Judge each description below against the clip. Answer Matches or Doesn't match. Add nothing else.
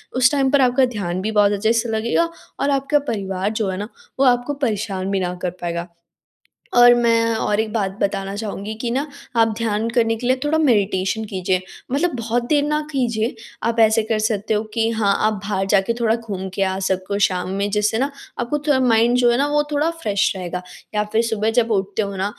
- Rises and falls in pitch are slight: Doesn't match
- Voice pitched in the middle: Doesn't match